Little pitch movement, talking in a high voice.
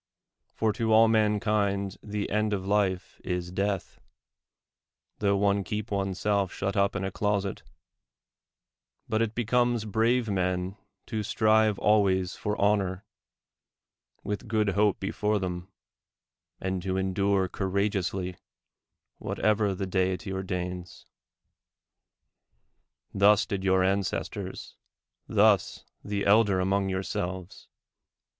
No: narrow, 2.0 semitones; low, 100 Hz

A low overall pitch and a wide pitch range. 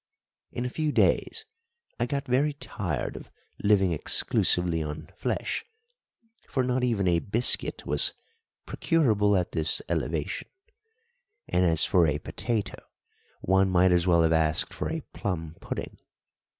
Yes: very low, 95 Hz; wide, 6.7 semitones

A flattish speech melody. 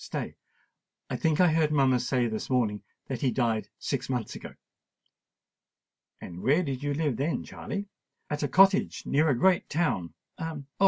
No: average, 4.6 semitones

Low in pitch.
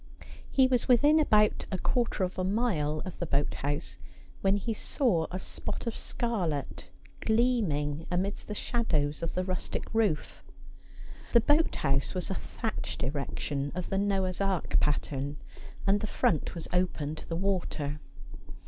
No: medium, 185 Hz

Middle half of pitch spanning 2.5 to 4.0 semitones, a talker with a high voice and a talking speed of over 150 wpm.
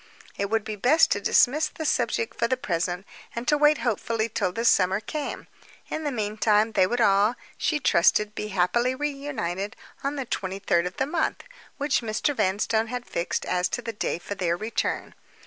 No: average, 5.1 semitones; high, 220 Hz; average, 190 wpm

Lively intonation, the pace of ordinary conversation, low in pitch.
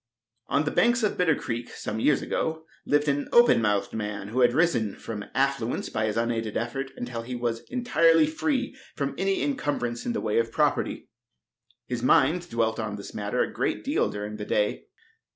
Yes: wide, 6.2 semitones; average, 190 wpm; low, 125 Hz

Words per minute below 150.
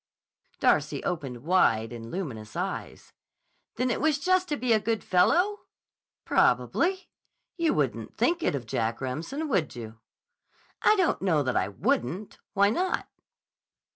Yes: average, 140 wpm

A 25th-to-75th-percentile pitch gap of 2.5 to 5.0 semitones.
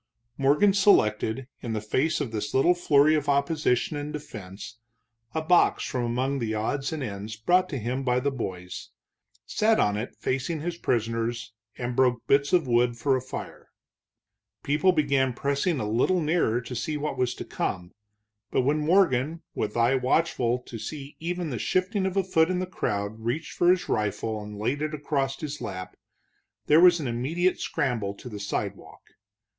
No: wide, 5.5 semitones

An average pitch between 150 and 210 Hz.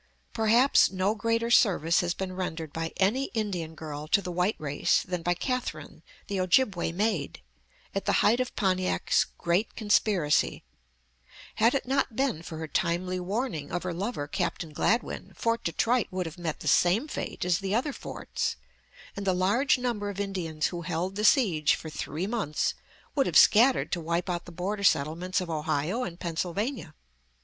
Yes: medium, 185 Hz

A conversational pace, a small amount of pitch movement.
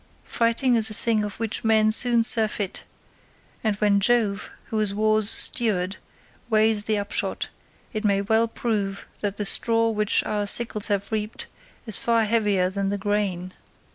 Yes: average, 160 wpm; narrow, 1.9 semitones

